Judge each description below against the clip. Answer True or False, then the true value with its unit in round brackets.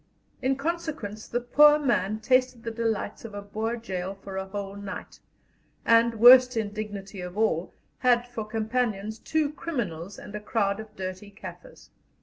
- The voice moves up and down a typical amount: True (3.3 semitones)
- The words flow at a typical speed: True (155 wpm)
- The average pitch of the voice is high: True (220 Hz)